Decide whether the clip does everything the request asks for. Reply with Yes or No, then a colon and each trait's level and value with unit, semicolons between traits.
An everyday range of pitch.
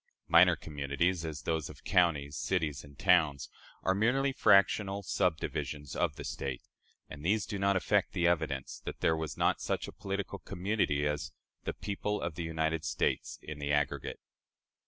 Yes: average, 4.6 semitones